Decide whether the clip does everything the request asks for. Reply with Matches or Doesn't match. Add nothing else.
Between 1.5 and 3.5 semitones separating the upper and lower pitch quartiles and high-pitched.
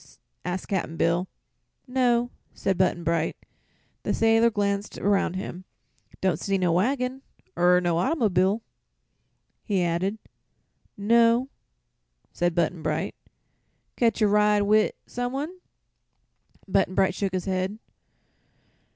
Doesn't match